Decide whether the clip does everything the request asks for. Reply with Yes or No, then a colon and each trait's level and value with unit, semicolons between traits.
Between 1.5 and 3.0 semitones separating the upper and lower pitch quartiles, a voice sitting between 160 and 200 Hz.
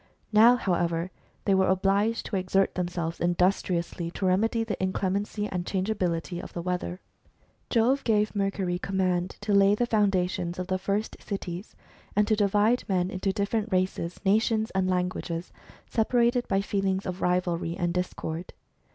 Yes: narrow, 2.6 semitones; high, 190 Hz